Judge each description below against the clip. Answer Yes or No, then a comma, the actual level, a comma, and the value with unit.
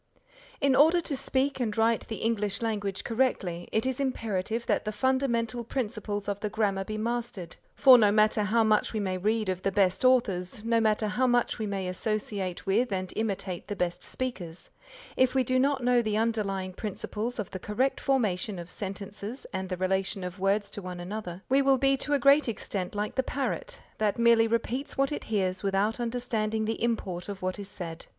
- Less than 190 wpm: No, average, 200 wpm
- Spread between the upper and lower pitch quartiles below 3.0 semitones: No, average, 3.9 semitones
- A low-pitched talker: No, high, 215 Hz